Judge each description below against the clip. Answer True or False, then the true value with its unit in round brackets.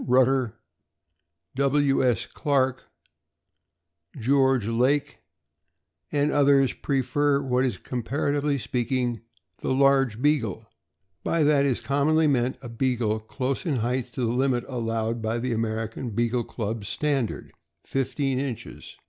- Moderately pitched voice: False (130 Hz)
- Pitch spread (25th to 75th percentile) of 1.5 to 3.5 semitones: True (3.0 semitones)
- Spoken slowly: True (130 wpm)